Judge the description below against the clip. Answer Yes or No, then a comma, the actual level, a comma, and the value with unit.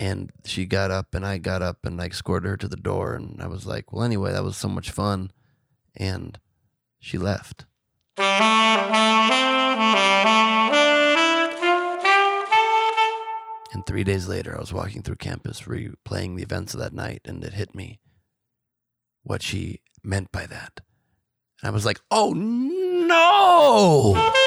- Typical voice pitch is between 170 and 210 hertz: No, low, 120 Hz